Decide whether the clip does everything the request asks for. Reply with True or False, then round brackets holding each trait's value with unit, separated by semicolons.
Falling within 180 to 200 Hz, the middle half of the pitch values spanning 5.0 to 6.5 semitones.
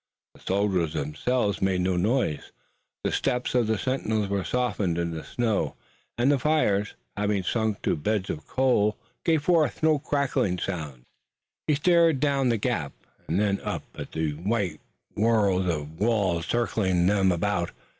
False (105 Hz; 5.6 semitones)